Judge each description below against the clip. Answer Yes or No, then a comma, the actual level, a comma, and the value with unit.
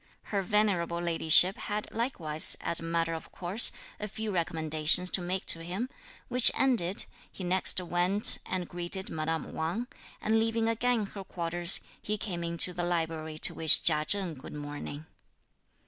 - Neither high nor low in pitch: Yes, medium, 175 Hz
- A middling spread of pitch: Yes, average, 3.8 semitones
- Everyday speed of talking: Yes, average, 160 wpm